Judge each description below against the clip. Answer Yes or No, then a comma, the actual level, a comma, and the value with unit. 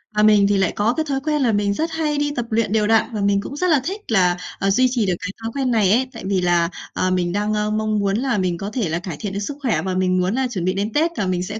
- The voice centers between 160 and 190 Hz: No, high, 210 Hz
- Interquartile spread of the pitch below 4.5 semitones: No, average, 4.9 semitones